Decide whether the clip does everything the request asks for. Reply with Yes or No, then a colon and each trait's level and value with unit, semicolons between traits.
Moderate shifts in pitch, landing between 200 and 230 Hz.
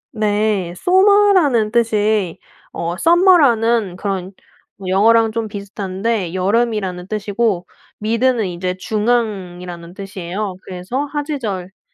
Yes: average, 4.0 semitones; high, 210 Hz